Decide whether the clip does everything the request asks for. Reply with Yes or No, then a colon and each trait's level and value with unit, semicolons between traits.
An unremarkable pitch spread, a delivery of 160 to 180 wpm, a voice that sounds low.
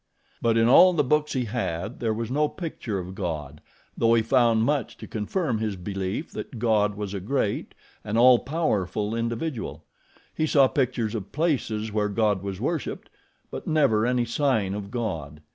Yes: average, 4.2 semitones; average, 175 wpm; low, 115 Hz